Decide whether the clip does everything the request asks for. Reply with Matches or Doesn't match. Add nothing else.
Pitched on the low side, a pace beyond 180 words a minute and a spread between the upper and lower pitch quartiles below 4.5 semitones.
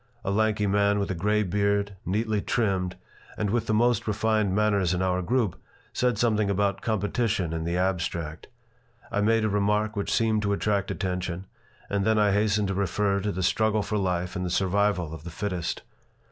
Matches